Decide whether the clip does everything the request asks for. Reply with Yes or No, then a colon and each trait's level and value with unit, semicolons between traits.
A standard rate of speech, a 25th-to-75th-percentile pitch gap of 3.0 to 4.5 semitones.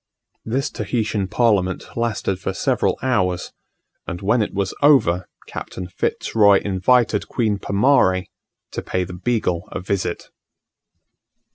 No: slow, 125 wpm; average, 4.1 semitones